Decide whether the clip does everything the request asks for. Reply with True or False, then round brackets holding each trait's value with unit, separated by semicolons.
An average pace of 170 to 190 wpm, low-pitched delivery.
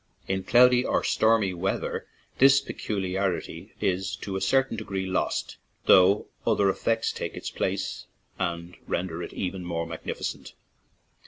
False (135 wpm; 95 Hz)